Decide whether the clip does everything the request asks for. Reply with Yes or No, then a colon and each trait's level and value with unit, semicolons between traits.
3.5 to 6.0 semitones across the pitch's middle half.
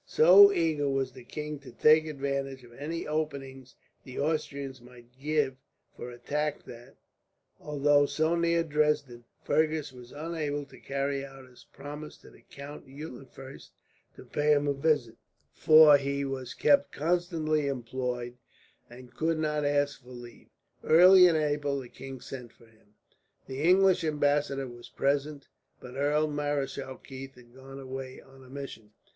No: narrow, 2.6 semitones